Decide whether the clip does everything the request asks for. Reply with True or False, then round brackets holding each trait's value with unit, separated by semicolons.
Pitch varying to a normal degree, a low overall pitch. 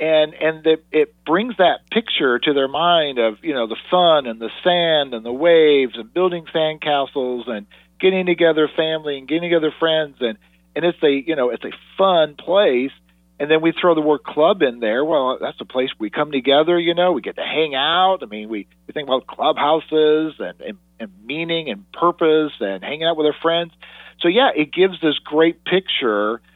False (4.4 semitones; 155 Hz)